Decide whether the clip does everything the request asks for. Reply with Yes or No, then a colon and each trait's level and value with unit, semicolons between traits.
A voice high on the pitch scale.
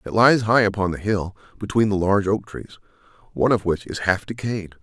No: low, 100 Hz